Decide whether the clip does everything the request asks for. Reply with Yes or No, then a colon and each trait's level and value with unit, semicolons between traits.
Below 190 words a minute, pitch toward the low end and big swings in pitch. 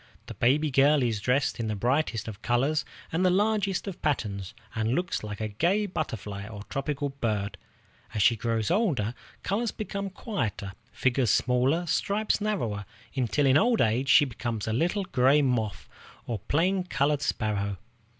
Yes: average, 160 wpm; low, 130 Hz; wide, 7.6 semitones